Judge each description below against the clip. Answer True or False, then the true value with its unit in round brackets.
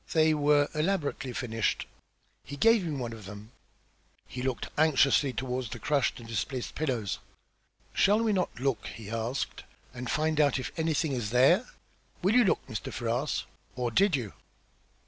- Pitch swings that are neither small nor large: True (4.7 semitones)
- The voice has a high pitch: False (135 Hz)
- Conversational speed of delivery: True (160 wpm)